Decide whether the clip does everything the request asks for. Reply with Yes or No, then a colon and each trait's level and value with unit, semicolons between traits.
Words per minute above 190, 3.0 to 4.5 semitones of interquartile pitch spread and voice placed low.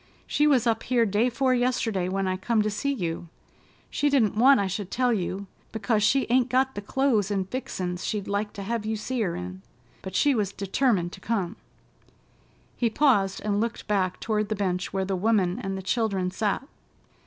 No: average, 200 wpm; average, 3.9 semitones; high, 210 Hz